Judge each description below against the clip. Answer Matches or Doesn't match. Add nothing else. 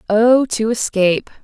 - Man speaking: Doesn't match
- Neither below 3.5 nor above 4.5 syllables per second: Matches